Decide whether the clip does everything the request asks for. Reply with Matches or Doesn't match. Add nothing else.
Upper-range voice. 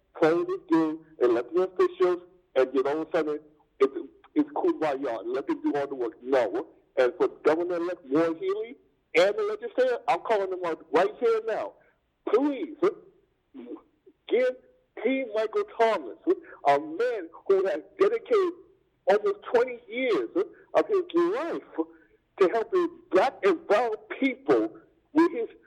Matches